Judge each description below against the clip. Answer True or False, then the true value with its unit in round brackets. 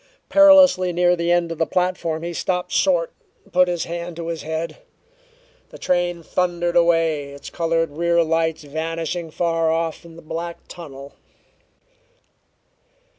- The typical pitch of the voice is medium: True (170 Hz)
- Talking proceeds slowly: False (145 wpm)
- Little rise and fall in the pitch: True (1.3 semitones)